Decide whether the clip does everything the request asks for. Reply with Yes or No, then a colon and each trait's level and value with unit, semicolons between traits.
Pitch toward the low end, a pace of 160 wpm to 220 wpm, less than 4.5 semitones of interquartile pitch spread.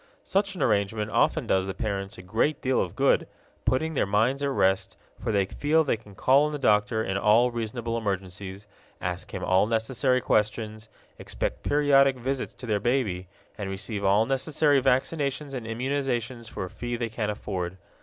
No: low, 115 Hz; average, 180 wpm; average, 4.8 semitones